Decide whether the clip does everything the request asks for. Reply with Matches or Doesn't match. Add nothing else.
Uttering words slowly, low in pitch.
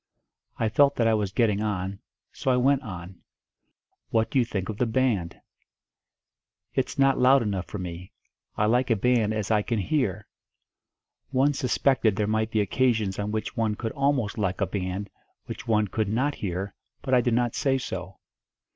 Doesn't match